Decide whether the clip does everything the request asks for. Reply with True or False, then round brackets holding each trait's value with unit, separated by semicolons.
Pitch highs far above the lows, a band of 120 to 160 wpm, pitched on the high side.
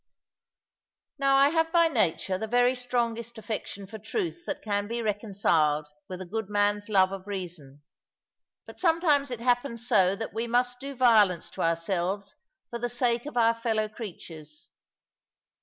False (4.1 semitones; 155 wpm; 225 Hz)